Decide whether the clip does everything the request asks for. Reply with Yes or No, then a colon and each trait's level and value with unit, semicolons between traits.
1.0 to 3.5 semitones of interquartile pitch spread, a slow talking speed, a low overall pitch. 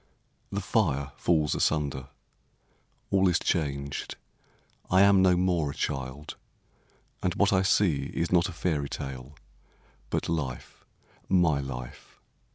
No: average, 4.8 semitones; slow, 125 wpm; very low, 80 Hz